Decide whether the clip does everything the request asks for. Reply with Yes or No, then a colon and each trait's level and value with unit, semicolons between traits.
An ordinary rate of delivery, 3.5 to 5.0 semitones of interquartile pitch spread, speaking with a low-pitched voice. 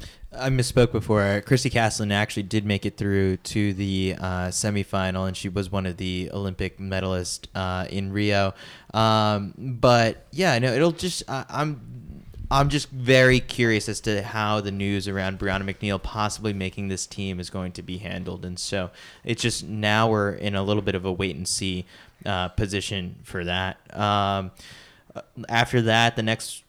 No: average, 180 wpm; average, 2.9 semitones; low, 100 Hz